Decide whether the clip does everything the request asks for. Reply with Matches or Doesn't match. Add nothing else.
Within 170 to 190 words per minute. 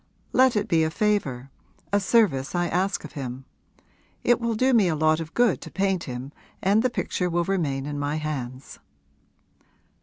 Matches